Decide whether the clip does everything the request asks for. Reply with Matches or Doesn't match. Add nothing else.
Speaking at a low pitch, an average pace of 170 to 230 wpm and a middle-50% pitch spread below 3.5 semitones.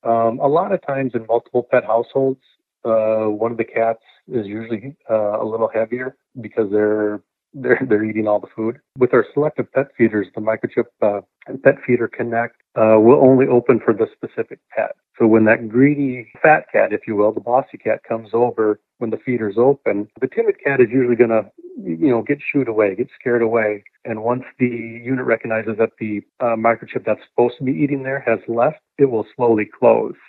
Matches